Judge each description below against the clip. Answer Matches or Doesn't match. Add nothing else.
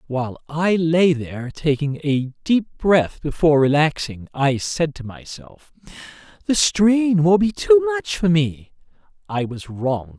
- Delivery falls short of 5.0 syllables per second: Matches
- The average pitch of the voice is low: Doesn't match